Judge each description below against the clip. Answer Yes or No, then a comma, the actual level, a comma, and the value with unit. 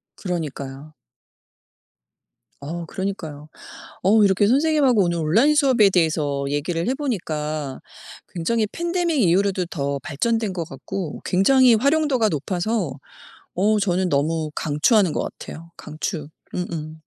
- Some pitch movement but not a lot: No, wide, 6.4 semitones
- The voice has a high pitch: No, medium, 180 Hz